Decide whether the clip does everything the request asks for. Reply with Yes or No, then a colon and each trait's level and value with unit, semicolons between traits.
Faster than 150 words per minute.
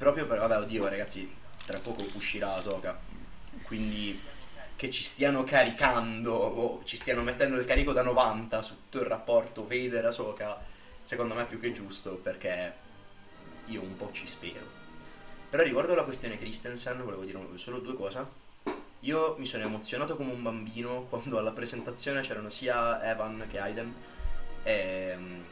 Yes: average, 160 wpm